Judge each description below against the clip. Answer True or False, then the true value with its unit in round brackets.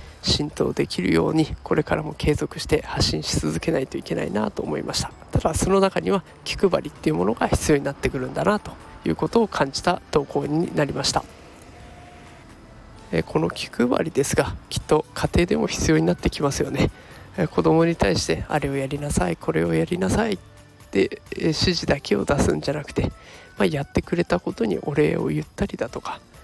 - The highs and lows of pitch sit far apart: False (4.8 semitones)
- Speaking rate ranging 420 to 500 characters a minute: False (375 characters per minute)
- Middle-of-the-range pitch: True (150 Hz)